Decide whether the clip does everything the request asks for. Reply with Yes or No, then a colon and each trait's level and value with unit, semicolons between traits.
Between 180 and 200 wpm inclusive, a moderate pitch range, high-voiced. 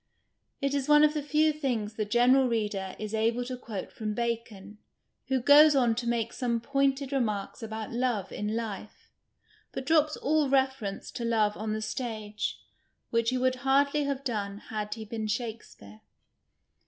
No: average, 165 wpm; average, 4.0 semitones; high, 235 Hz